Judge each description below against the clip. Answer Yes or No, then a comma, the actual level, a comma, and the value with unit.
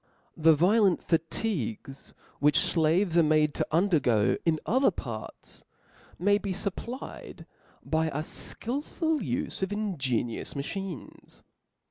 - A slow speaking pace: Yes, slow, 115 wpm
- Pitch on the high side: No, medium, 170 Hz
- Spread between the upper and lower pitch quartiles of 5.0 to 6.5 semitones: Yes, average, 5.3 semitones